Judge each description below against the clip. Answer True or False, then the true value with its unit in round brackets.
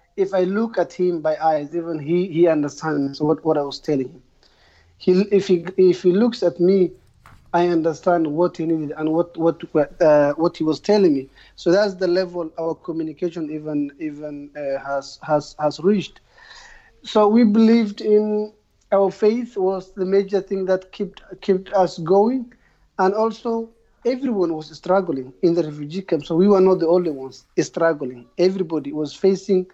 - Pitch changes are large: False (3.9 semitones)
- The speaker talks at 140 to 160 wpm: False (175 wpm)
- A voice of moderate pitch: True (175 Hz)